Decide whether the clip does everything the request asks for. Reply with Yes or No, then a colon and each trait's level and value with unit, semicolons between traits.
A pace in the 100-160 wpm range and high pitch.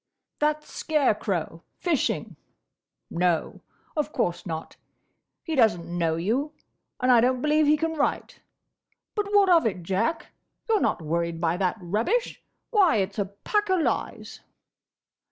Yes: average, 140 wpm; high, 230 Hz